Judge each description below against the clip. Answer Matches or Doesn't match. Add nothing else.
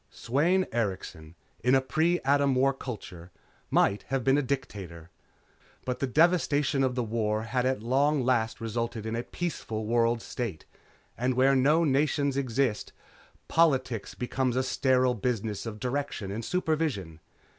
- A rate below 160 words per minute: Matches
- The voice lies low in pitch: Matches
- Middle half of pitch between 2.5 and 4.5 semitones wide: Matches